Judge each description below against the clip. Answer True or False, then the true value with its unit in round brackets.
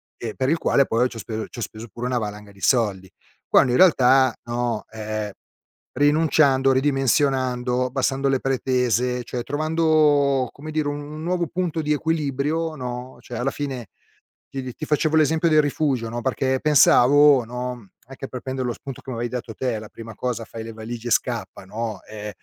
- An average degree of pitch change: True (3.6 semitones)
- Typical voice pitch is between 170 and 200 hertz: False (130 Hz)